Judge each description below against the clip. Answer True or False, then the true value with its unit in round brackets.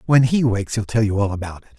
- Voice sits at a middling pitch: False (110 Hz)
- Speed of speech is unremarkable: False (305 wpm)